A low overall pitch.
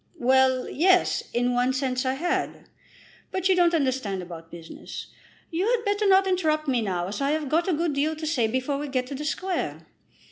No: very high, 280 Hz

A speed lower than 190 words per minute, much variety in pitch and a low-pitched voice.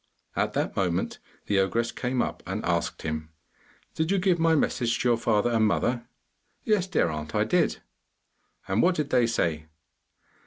Yes: average, 170 wpm; wide, 8.2 semitones; low, 115 Hz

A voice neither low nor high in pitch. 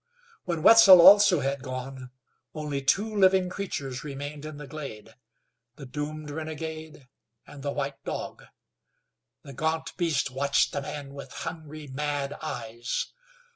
Yes: medium, 145 Hz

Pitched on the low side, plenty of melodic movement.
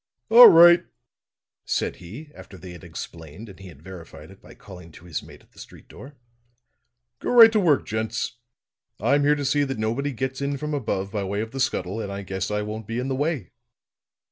Yes: low, 110 Hz; wide, 6.8 semitones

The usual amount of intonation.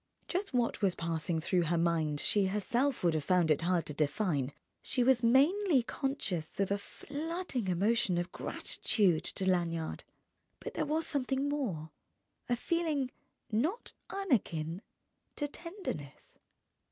No: wide, 8.9 semitones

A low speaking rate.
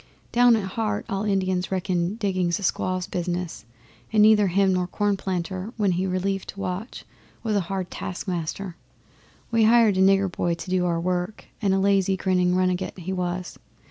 No: average, 175 wpm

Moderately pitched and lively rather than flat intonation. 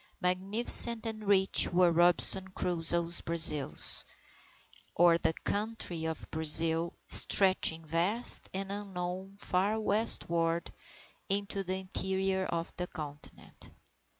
No: medium, 180 Hz; average, 2.9 semitones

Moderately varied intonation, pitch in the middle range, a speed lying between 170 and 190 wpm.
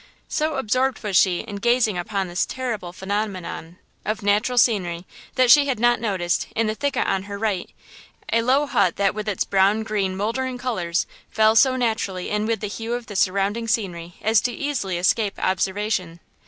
No: average, 3.7 semitones; high, 210 Hz; average, 180 wpm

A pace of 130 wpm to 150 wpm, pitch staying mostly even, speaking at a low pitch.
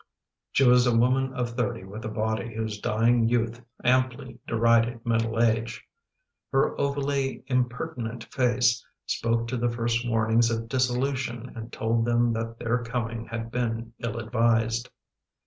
Yes: average, 145 wpm; narrow, 1.4 semitones; low, 115 Hz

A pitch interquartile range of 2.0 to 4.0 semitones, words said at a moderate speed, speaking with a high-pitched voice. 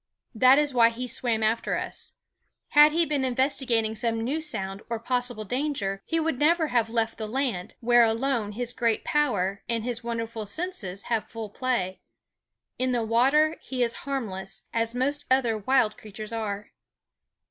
Yes: average, 3.3 semitones; average, 165 wpm; high, 235 Hz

